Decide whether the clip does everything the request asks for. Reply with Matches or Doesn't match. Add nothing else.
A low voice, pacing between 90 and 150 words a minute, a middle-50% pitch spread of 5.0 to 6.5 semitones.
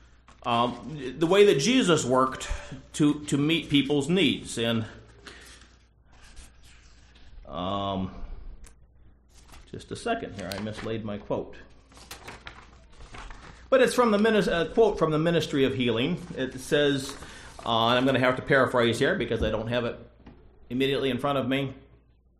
Matches